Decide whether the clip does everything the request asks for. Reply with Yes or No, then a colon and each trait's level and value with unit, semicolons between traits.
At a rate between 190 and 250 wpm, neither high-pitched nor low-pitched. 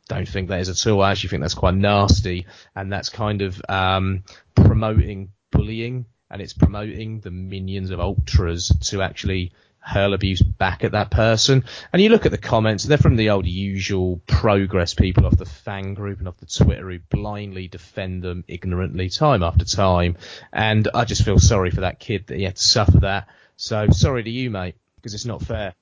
No: average, 200 wpm; low, 100 Hz